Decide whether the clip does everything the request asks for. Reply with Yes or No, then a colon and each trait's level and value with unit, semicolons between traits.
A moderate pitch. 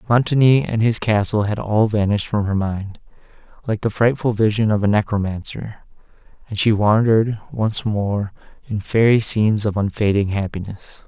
No: low, 105 Hz